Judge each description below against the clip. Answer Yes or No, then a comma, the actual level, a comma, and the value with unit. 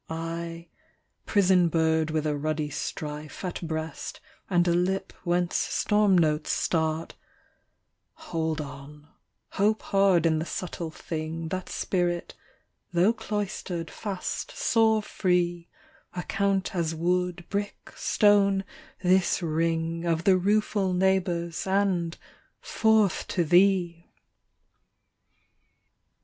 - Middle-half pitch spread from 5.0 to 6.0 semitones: No, average, 2.8 semitones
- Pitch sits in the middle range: Yes, medium, 175 Hz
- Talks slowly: Yes, slow, 110 wpm